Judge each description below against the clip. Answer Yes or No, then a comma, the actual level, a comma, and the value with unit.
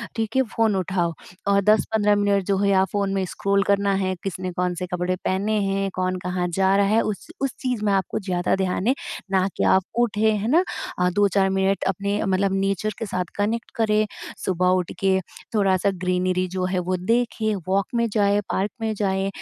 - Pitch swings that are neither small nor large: No, narrow, 2.0 semitones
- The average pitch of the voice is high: Yes, high, 195 Hz